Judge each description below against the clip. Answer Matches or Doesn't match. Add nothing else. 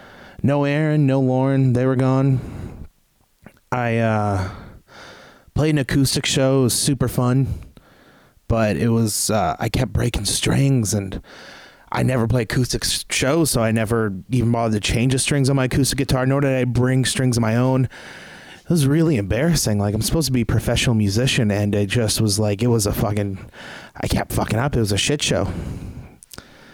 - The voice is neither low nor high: Doesn't match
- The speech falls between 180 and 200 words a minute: Matches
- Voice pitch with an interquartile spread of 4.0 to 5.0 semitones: Doesn't match